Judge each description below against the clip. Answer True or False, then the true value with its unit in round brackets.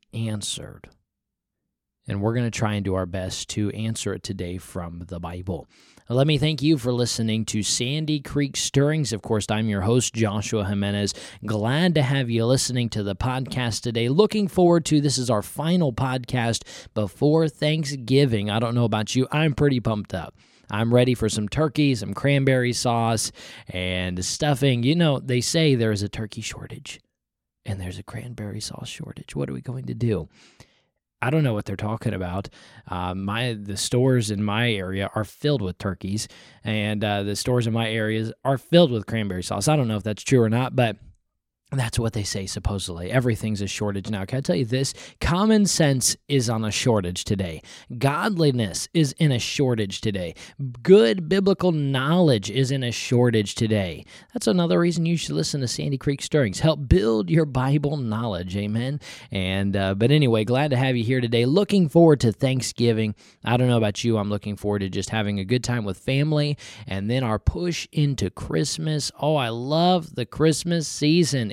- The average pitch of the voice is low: True (120 Hz)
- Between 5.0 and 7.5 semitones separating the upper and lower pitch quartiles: True (5.3 semitones)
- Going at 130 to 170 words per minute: False (190 wpm)